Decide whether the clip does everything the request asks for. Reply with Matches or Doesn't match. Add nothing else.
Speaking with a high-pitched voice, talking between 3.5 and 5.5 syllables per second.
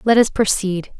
Matches